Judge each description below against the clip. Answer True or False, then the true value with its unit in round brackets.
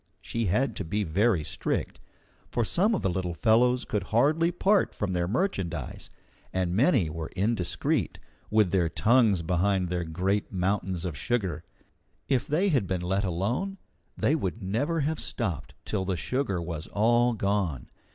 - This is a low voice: True (100 Hz)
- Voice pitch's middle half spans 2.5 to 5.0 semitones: False (5.5 semitones)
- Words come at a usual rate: True (160 wpm)